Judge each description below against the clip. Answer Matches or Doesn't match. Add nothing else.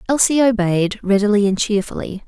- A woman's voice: Matches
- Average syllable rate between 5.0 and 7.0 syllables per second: Matches